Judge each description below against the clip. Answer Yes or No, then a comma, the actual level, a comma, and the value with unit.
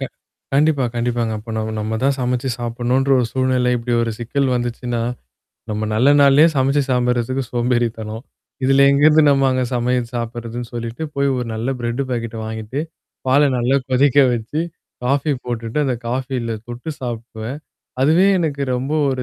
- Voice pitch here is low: Yes, low, 125 Hz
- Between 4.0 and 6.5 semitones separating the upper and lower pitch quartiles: No, narrow, 2.5 semitones